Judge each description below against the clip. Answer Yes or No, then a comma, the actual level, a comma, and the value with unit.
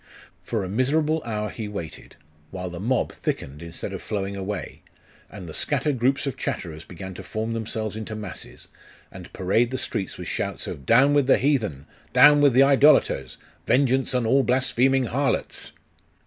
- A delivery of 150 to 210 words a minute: Yes, average, 170 wpm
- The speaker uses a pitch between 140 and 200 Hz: No, low, 115 Hz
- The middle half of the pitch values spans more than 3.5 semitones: Yes, wide, 5.6 semitones